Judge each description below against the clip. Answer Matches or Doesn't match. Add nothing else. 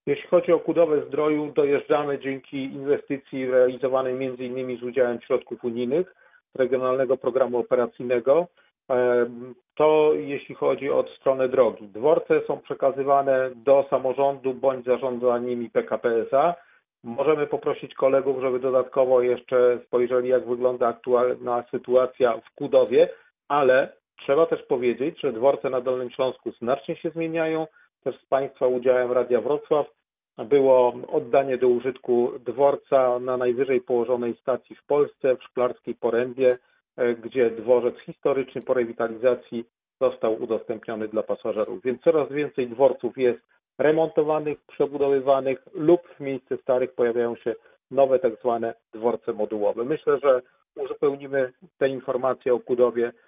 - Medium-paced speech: Matches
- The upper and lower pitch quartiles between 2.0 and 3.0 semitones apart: Doesn't match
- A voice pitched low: Matches